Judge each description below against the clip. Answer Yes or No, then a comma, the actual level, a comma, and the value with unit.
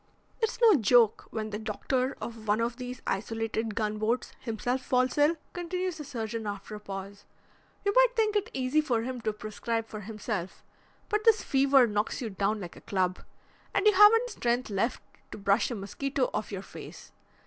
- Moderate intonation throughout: Yes, average, 4.7 semitones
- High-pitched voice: Yes, high, 230 Hz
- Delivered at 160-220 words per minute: Yes, average, 180 wpm